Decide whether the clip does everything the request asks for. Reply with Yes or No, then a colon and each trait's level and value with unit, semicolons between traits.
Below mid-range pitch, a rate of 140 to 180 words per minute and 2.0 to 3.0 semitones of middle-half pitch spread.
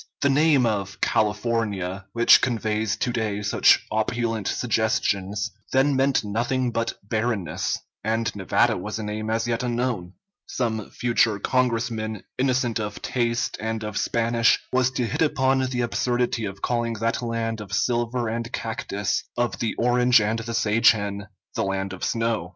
Yes: low, 115 Hz; average, 155 wpm; narrow, 2.4 semitones